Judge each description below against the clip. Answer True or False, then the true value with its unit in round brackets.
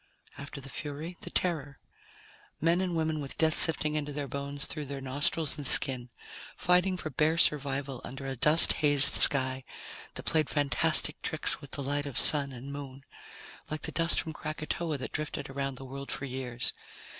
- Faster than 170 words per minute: True (180 wpm)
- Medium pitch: True (145 Hz)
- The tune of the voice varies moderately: False (2.3 semitones)